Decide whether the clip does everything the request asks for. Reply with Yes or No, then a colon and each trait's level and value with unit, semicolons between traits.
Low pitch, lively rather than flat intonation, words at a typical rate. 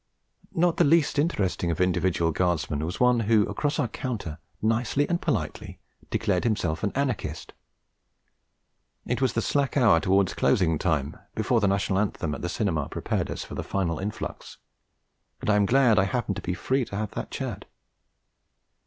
Yes: low, 105 Hz; wide, 5.7 semitones; average, 170 wpm